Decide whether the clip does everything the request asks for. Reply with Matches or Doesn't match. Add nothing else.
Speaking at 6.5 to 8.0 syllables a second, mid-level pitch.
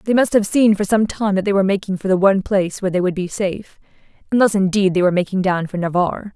Doesn't match